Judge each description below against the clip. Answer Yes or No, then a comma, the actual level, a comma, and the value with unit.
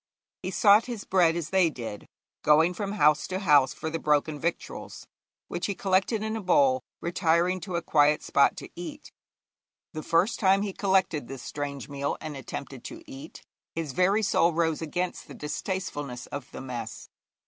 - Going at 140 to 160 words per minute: No, average, 175 wpm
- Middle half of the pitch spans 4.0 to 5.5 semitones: Yes, average, 4.6 semitones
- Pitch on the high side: No, medium, 170 Hz